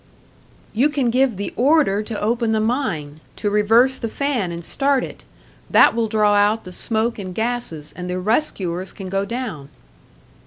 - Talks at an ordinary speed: Yes, average, 170 wpm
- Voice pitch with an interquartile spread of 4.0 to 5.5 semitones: Yes, average, 4.3 semitones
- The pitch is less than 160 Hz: No, high, 220 Hz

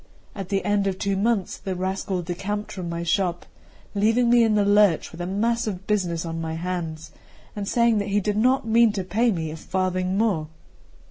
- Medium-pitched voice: No, high, 195 Hz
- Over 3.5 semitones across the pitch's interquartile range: No, average, 3.1 semitones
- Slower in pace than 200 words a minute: No, fast, 205 wpm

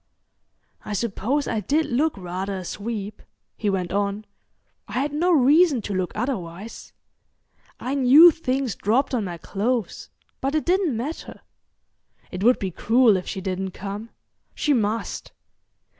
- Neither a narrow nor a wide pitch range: No, wide, 5.8 semitones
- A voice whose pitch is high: Yes, high, 225 Hz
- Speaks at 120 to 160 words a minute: Yes, average, 145 wpm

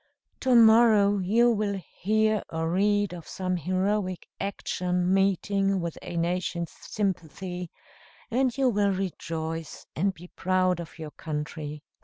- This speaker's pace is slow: Yes, slow, 130 wpm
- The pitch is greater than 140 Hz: Yes, medium, 185 Hz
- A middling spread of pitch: Yes, average, 3.1 semitones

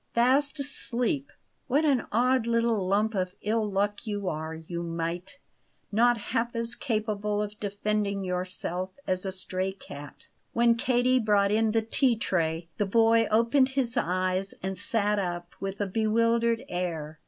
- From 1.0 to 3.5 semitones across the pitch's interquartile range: No, average, 3.9 semitones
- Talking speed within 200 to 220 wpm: No, average, 155 wpm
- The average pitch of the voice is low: No, high, 210 Hz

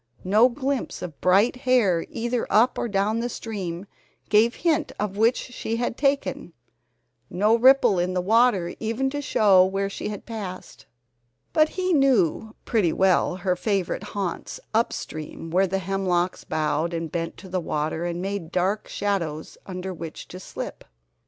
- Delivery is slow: No, average, 160 wpm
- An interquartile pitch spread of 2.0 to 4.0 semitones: No, average, 4.4 semitones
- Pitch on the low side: No, high, 195 Hz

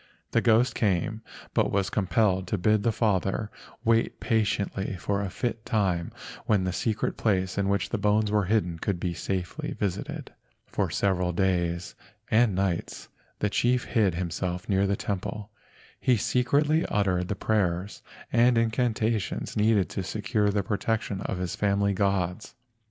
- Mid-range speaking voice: No, low, 100 Hz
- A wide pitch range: No, average, 2.9 semitones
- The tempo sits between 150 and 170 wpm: Yes, average, 155 wpm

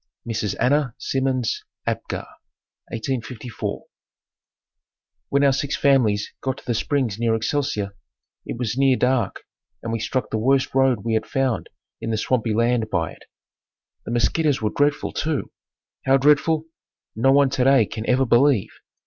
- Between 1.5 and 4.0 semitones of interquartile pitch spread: Yes, average, 3.3 semitones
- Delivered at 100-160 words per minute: Yes, average, 150 wpm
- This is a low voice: Yes, low, 125 Hz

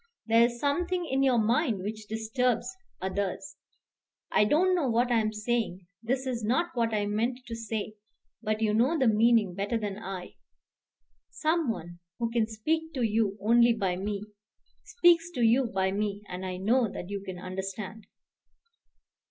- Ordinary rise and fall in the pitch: Yes, average, 3.5 semitones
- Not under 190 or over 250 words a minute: No, average, 165 wpm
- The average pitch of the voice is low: No, high, 225 Hz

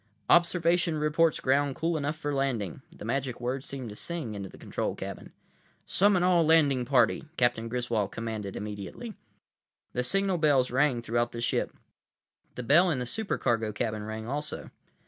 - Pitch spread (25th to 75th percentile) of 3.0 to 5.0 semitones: No, wide, 5.5 semitones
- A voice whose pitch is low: Yes, low, 130 Hz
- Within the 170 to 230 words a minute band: No, average, 160 wpm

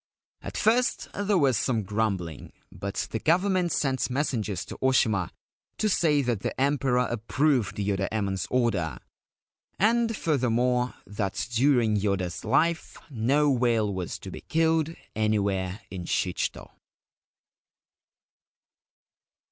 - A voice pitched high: No, low, 120 Hz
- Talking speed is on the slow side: Yes, slow, 115 wpm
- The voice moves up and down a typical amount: No, wide, 6.3 semitones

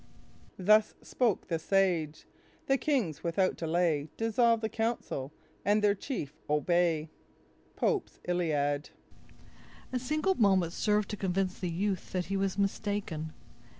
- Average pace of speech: No, slow, 125 wpm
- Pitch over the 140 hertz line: Yes, high, 190 Hz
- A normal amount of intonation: Yes, average, 4.5 semitones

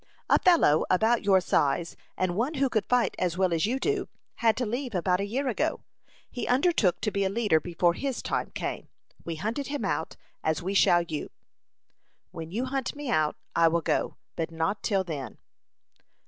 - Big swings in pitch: Yes, wide, 6.7 semitones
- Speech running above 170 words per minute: Yes, average, 190 wpm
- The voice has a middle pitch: No, high, 195 Hz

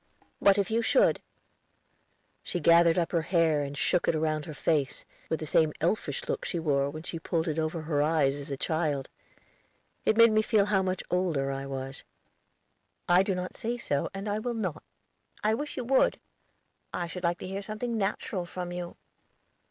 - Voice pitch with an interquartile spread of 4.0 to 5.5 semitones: Yes, average, 4.3 semitones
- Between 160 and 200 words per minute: Yes, average, 190 wpm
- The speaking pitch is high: No, medium, 170 Hz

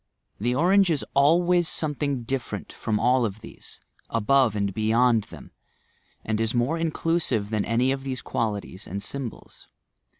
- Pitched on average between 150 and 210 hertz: No, low, 125 Hz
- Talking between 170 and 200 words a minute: No, average, 145 wpm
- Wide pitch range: No, average, 4.8 semitones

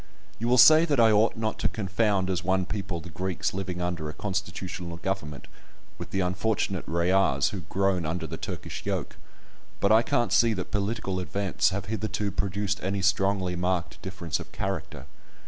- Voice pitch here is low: Yes, very low, 95 Hz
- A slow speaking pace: No, average, 175 wpm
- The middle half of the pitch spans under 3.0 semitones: Yes, narrow, 2.4 semitones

